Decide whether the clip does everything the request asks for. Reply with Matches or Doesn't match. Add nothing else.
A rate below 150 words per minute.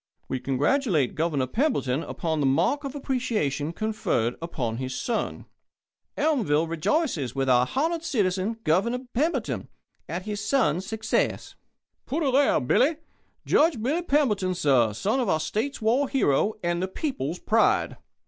Matches